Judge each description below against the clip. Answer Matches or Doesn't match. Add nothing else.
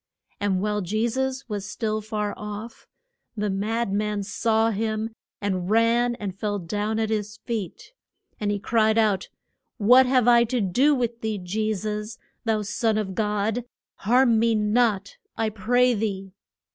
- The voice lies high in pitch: Matches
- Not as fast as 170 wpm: Matches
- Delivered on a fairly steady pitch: Matches